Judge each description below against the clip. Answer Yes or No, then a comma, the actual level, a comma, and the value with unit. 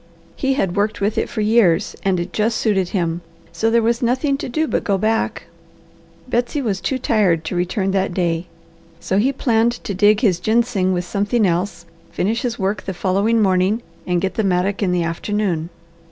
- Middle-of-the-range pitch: No, high, 200 Hz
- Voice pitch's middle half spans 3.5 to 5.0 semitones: Yes, average, 3.9 semitones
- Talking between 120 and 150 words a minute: No, average, 195 wpm